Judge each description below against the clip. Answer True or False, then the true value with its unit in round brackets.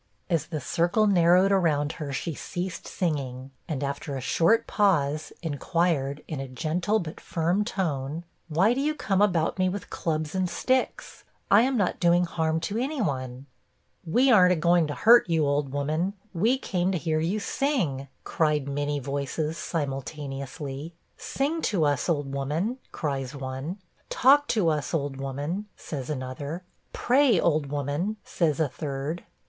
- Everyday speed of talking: True (160 wpm)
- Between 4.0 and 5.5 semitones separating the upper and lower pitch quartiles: True (4.8 semitones)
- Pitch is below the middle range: False (160 Hz)